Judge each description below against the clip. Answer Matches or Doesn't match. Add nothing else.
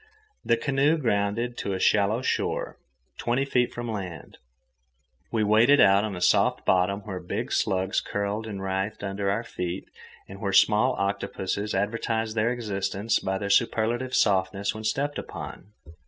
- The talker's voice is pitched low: Matches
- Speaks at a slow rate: Doesn't match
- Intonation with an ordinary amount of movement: Matches